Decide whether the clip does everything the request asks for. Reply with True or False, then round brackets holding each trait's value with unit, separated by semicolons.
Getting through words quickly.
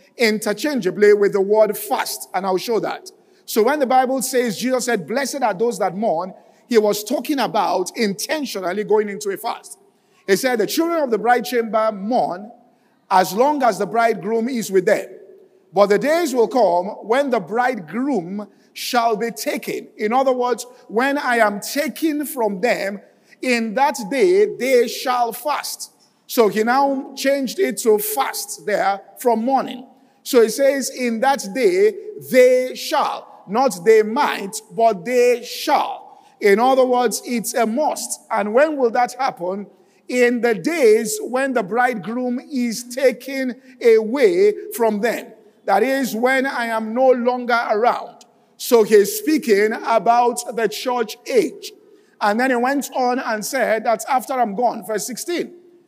False (160 wpm)